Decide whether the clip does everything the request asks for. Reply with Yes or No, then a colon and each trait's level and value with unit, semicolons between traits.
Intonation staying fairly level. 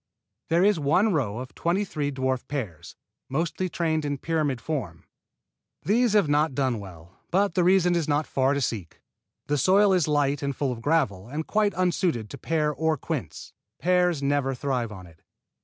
No: average, 4.9 semitones